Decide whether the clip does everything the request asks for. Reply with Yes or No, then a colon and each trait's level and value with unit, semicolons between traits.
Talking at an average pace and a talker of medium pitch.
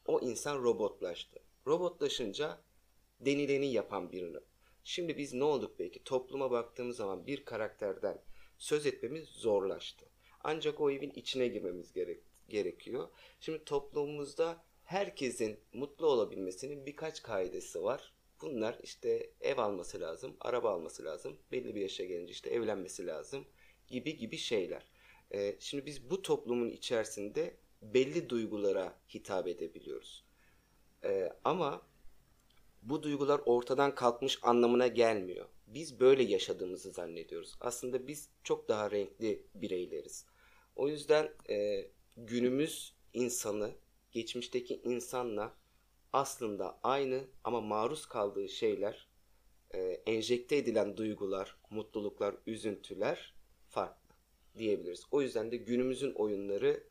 Yes: average, 115 wpm; medium, 155 Hz